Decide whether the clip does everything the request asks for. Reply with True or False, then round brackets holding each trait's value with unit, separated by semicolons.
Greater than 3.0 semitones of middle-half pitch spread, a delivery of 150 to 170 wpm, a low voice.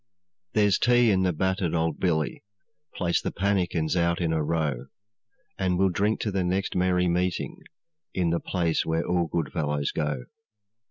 False (2.6 semitones; 165 wpm; 90 Hz)